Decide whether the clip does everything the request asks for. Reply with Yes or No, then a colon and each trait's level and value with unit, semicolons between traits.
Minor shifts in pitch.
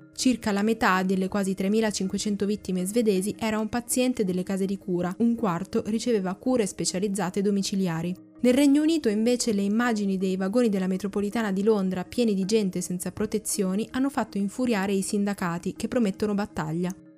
No: average, 3.1 semitones